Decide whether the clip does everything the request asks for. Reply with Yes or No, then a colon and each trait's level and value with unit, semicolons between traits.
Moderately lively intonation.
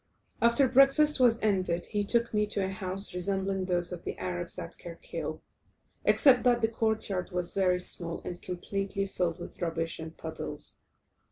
Yes: average, 4.0 semitones